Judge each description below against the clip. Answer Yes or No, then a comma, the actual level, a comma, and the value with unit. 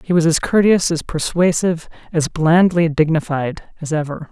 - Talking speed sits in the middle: Yes, average, 155 wpm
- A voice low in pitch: No, medium, 160 Hz